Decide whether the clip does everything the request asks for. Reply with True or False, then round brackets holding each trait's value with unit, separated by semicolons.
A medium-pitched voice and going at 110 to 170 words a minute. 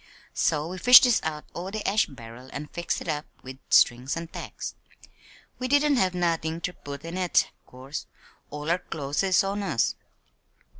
False (165 Hz; 180 wpm)